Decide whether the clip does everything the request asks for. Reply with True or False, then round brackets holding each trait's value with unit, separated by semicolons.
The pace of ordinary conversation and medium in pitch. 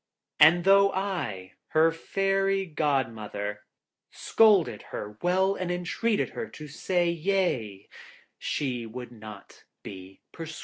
False (120 wpm; 160 Hz)